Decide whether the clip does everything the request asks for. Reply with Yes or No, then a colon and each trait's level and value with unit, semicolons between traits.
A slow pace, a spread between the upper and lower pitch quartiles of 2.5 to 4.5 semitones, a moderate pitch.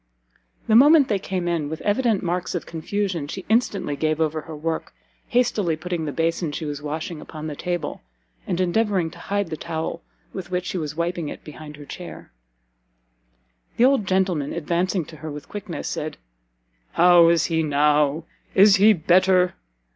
No: average, 170 wpm; average, 3.4 semitones; medium, 170 Hz